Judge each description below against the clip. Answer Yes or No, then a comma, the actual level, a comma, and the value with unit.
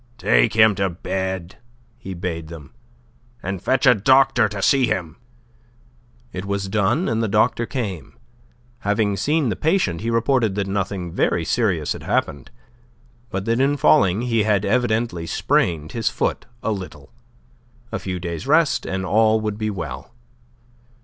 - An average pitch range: Yes, average, 4.0 semitones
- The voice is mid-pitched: No, low, 100 Hz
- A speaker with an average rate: Yes, average, 155 wpm